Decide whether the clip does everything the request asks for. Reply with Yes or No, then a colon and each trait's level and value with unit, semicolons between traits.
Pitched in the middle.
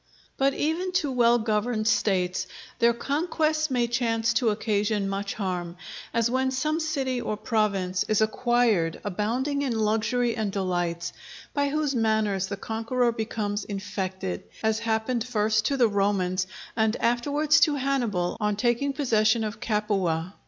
No: high, 220 Hz